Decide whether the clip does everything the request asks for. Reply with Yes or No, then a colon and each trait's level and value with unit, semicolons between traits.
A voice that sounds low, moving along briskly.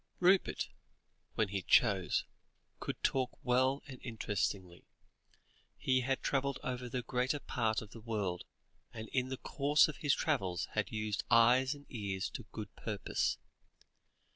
No: low, 120 Hz; average, 140 wpm